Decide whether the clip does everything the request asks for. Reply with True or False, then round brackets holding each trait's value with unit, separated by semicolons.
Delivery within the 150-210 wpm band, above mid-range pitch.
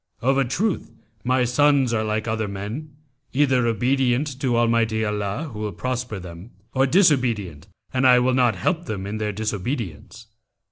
False (160 wpm; 120 Hz)